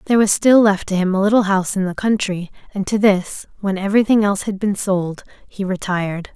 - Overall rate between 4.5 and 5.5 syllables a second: No, 5.9 syllables/s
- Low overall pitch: No, high, 200 Hz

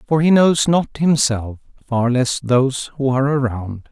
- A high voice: No, low, 130 Hz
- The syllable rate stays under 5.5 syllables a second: Yes, 4.5 syllables/s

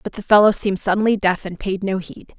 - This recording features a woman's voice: Yes, female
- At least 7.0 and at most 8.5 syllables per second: No, 6.0 syllables/s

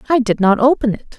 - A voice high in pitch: Yes, high, 235 Hz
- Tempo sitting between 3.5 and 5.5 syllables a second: No, 6.1 syllables/s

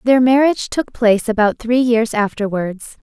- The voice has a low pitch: No, high, 230 Hz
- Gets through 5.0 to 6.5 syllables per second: No, 4.8 syllables/s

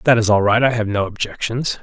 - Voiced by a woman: No, male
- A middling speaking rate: No, fast, 265 wpm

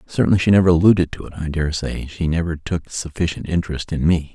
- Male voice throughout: Yes, male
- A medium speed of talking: No, fast, 220 wpm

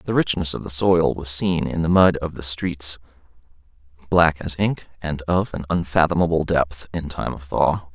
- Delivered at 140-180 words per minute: No, average, 190 wpm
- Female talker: No, male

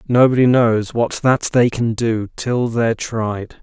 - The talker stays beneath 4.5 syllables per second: Yes, 3.8 syllables/s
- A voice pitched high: No, low, 115 Hz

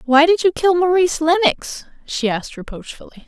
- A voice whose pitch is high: Yes, very high, 315 Hz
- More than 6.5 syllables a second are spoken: No, 5.5 syllables/s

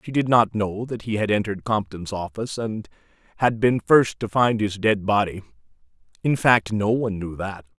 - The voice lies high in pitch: No, low, 105 Hz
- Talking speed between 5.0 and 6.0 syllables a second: Yes, 5.2 syllables/s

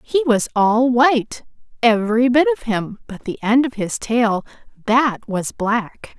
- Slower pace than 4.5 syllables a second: Yes, 4.0 syllables/s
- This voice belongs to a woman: Yes, female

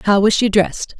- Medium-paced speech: No, fast, 240 wpm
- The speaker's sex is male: No, female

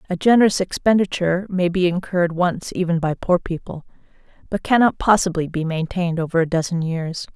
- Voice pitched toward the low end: No, medium, 175 Hz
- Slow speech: No, average, 165 wpm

